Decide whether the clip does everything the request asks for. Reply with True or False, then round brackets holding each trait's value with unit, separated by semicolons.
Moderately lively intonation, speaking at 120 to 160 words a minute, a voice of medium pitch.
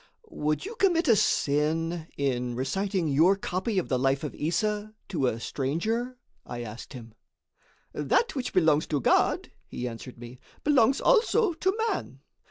False (8.9 semitones; 155 wpm; 165 Hz)